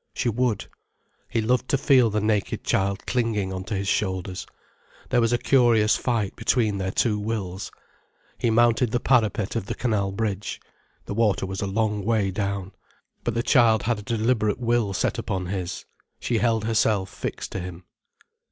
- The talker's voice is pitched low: Yes, low, 110 Hz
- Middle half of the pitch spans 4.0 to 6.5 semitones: No, average, 3.1 semitones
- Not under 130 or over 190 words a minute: Yes, average, 175 wpm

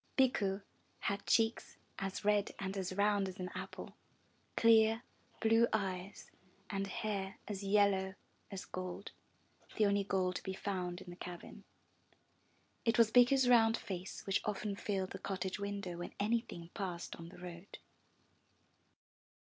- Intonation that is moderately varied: No, narrow, 2.2 semitones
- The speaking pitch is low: No, high, 195 Hz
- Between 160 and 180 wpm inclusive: No, average, 145 wpm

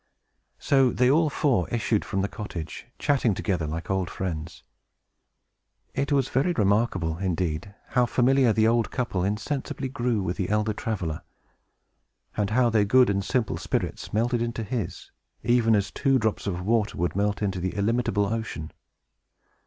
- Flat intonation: No, average, 4.3 semitones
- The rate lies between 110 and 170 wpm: Yes, average, 155 wpm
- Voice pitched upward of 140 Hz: No, low, 105 Hz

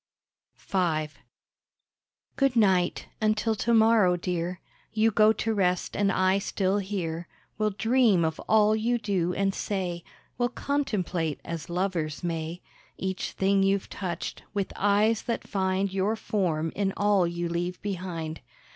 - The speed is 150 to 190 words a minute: No, average, 140 wpm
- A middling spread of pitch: Yes, average, 3.4 semitones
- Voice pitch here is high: Yes, high, 195 Hz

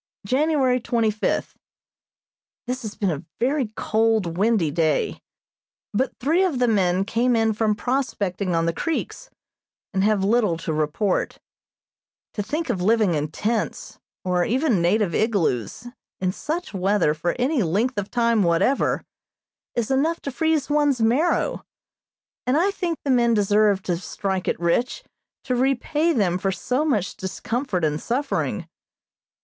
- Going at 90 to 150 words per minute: Yes, average, 145 wpm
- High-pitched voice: Yes, high, 220 Hz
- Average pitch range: No, wide, 5.7 semitones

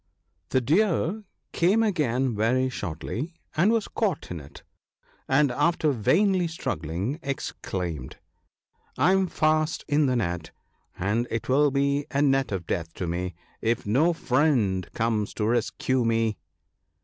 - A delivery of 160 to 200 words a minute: No, average, 140 wpm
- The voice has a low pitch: Yes, low, 130 Hz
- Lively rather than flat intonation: Yes, wide, 6.8 semitones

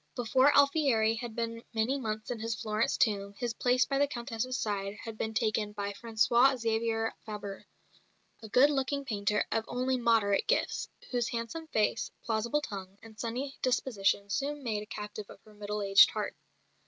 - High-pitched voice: Yes, high, 225 Hz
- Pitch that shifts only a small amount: No, average, 3.2 semitones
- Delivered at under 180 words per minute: Yes, average, 170 wpm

